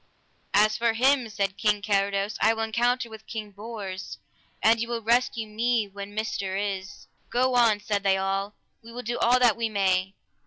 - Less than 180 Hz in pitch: No, high, 215 Hz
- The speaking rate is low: No, average, 185 wpm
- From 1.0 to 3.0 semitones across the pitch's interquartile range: Yes, average, 2.7 semitones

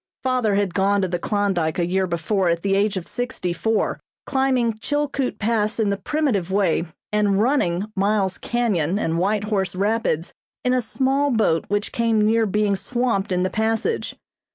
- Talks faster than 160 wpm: Yes, average, 175 wpm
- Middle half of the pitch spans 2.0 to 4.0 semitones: Yes, average, 3.5 semitones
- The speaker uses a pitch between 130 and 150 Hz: No, high, 205 Hz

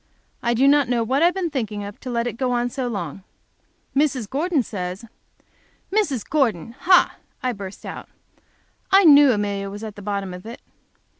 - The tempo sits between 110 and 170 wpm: No, average, 195 wpm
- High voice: Yes, high, 240 Hz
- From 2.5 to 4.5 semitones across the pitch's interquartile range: No, wide, 5.5 semitones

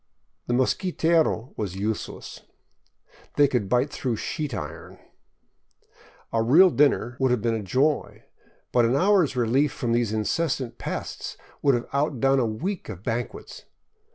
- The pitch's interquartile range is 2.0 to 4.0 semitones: No, average, 4.4 semitones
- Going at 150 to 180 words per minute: No, average, 140 wpm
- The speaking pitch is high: No, low, 125 Hz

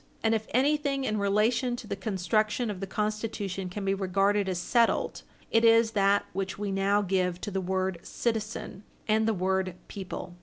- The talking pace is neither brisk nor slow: Yes, average, 180 wpm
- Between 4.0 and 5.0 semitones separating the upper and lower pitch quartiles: No, average, 2.7 semitones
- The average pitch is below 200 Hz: No, high, 205 Hz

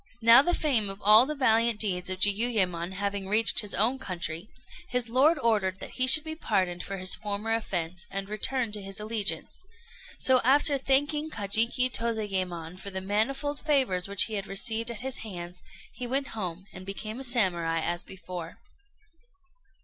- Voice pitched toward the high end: Yes, high, 210 Hz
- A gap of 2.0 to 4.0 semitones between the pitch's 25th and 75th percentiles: No, average, 4.8 semitones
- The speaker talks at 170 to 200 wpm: Yes, average, 175 wpm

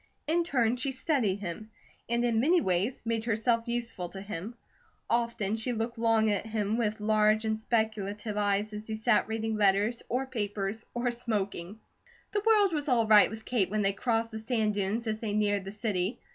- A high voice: Yes, high, 220 Hz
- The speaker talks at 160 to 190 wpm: Yes, average, 185 wpm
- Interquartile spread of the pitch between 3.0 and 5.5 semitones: No, narrow, 2.4 semitones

